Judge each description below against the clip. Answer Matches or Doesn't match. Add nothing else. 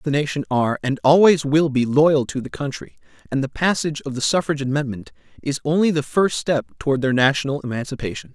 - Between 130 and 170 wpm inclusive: Doesn't match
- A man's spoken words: Matches